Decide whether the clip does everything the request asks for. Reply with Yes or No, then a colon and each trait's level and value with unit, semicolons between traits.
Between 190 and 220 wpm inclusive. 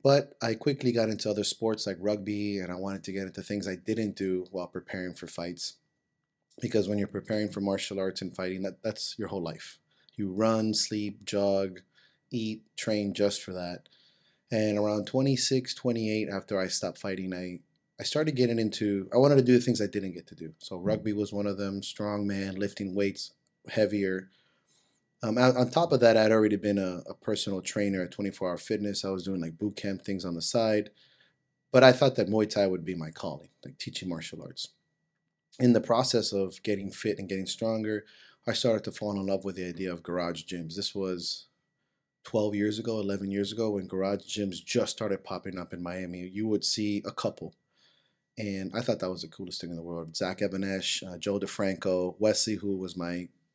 Yes: fast, 205 wpm